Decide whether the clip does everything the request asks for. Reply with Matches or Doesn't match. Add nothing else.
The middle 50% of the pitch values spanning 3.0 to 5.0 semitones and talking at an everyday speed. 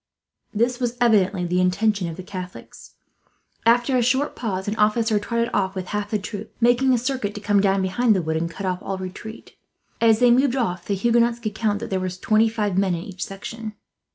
Doesn't match